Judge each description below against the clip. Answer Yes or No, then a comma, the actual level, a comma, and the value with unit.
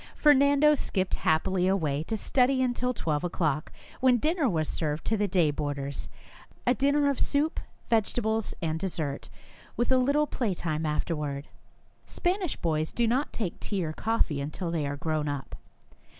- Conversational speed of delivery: Yes, average, 160 wpm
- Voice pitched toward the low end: No, high, 190 Hz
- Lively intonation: Yes, wide, 8.6 semitones